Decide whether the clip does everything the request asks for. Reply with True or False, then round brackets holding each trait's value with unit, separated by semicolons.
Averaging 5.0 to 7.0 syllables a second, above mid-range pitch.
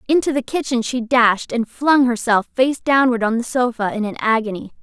True (5.2 syllables/s; 240 Hz)